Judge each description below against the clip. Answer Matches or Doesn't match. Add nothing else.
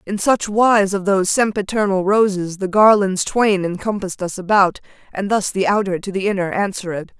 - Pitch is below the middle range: Doesn't match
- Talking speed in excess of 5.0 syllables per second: Matches